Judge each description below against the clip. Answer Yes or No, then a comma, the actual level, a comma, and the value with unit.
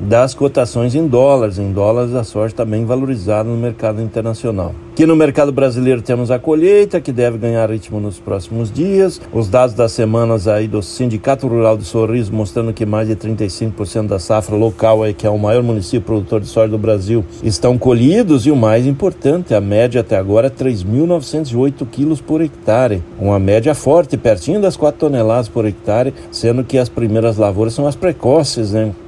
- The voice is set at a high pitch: No, low, 115 Hz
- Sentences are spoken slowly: No, fast, 185 wpm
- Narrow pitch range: No, average, 3.6 semitones